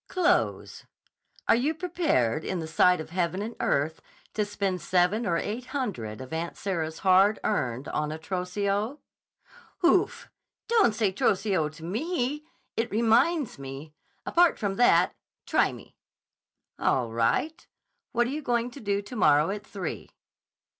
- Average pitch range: No, wide, 7.0 semitones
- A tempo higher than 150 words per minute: No, average, 140 wpm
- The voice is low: No, high, 200 Hz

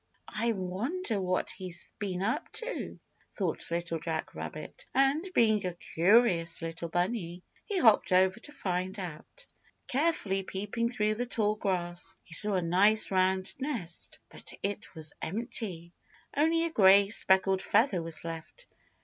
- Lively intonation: No, average, 4.7 semitones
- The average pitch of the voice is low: No, high, 195 Hz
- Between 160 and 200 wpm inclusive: No, average, 145 wpm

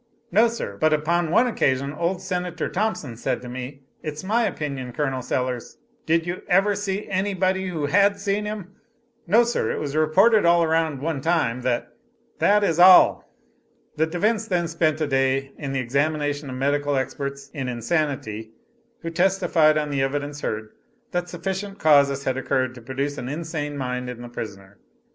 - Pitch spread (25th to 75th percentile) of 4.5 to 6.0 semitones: Yes, average, 5.2 semitones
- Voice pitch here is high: No, medium, 155 Hz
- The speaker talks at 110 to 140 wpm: No, average, 175 wpm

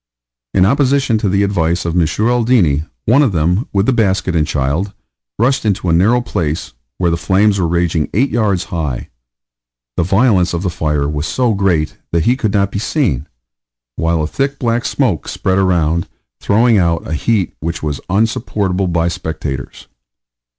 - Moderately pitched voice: No, very low, 95 Hz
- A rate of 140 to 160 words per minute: No, average, 170 wpm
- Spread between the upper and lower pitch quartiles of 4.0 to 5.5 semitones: Yes, average, 5.0 semitones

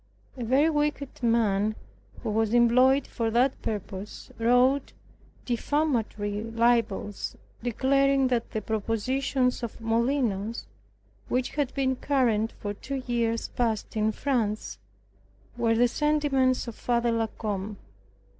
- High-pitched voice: Yes, high, 235 Hz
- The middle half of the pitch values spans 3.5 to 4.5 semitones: No, average, 3.1 semitones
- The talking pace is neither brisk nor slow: No, slow, 115 wpm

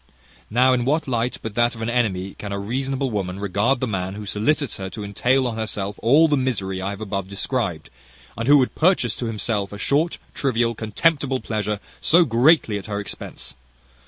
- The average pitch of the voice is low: Yes, low, 115 Hz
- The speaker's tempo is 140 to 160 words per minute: No, average, 200 wpm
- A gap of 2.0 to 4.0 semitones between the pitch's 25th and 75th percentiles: No, average, 4.4 semitones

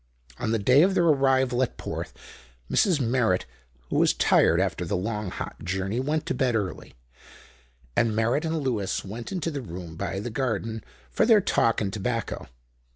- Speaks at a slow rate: No, average, 175 wpm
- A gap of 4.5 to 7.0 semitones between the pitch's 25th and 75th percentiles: Yes, average, 5.2 semitones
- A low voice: Yes, low, 115 Hz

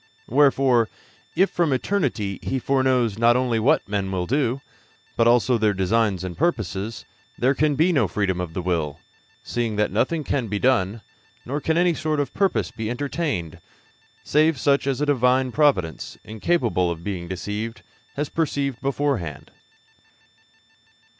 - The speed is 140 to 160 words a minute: Yes, average, 150 wpm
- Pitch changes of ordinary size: No, wide, 5.9 semitones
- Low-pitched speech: Yes, low, 120 Hz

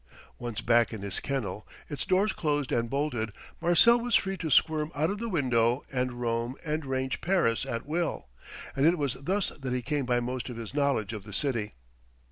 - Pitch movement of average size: Yes, average, 5.0 semitones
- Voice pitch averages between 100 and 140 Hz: Yes, low, 135 Hz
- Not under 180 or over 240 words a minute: Yes, average, 200 wpm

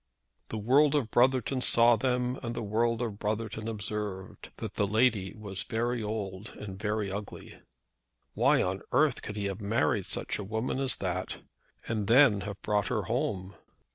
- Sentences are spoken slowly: No, average, 170 wpm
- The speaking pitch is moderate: No, low, 110 Hz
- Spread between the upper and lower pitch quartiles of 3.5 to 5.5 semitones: No, average, 3.1 semitones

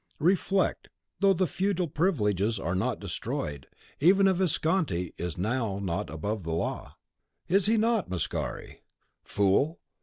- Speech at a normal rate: No, slow, 130 wpm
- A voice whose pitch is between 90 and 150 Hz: Yes, low, 135 Hz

